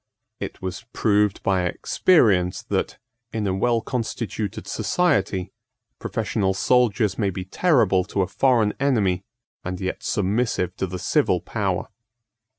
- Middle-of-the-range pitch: No, low, 100 Hz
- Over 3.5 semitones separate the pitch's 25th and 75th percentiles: Yes, average, 4.0 semitones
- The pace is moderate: No, slow, 130 wpm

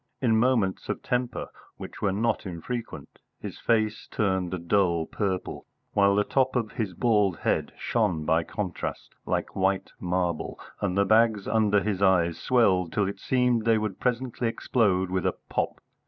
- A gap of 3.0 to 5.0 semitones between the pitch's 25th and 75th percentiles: Yes, average, 3.7 semitones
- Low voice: Yes, low, 100 Hz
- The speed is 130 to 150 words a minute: No, average, 165 wpm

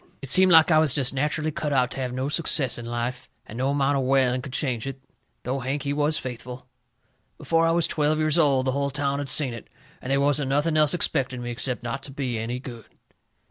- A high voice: No, low, 135 Hz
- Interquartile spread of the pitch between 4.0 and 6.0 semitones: No, average, 2.7 semitones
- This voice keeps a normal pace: No, fast, 240 wpm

